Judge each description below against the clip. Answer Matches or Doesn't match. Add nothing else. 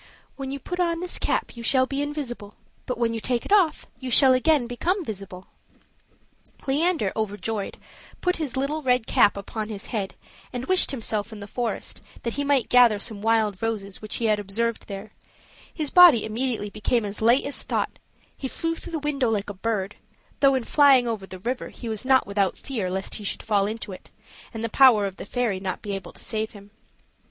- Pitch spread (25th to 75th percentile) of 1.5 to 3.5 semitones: Doesn't match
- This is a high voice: Matches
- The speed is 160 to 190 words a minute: Doesn't match